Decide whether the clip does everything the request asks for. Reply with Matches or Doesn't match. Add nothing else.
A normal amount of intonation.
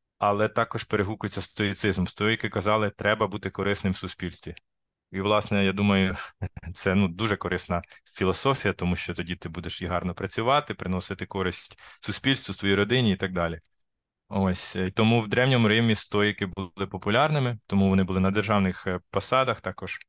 Doesn't match